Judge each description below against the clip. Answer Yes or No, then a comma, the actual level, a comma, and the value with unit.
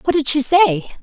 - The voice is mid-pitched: No, very high, 285 Hz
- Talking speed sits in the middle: No, fast, 235 wpm